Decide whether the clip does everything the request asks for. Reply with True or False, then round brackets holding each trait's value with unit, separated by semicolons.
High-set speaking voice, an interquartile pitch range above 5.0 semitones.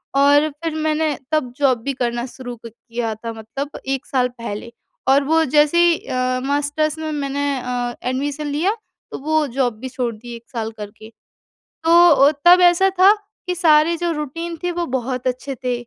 False (280 Hz; 4.0 semitones)